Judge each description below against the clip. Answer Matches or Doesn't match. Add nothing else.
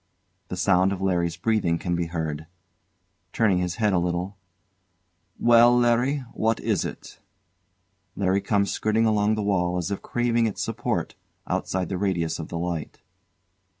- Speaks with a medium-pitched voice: Doesn't match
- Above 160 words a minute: Doesn't match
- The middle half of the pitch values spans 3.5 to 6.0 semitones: Matches